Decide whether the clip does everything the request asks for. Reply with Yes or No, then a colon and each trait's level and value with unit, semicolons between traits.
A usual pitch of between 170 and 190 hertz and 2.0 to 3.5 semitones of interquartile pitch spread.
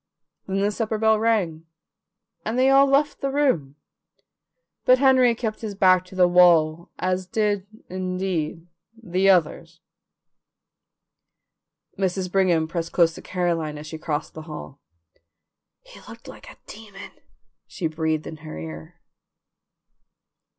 No: medium, 185 Hz; average, 4.9 semitones